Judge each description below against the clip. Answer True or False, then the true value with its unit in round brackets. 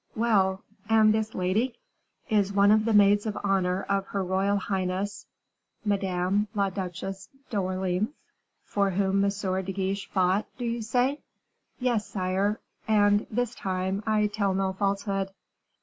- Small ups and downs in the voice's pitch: True (1.9 semitones)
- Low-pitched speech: False (200 Hz)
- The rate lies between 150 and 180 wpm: False (140 wpm)